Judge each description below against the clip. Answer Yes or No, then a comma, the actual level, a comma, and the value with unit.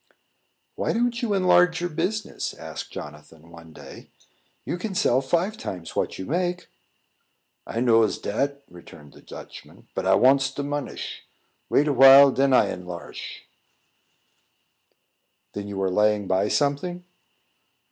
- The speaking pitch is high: No, low, 135 Hz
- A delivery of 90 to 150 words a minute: Yes, slow, 135 wpm